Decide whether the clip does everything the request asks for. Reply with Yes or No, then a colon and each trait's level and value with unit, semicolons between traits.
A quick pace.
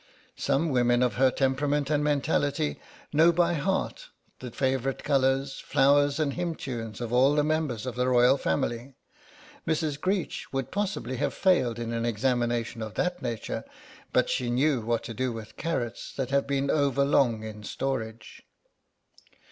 No: average, 160 wpm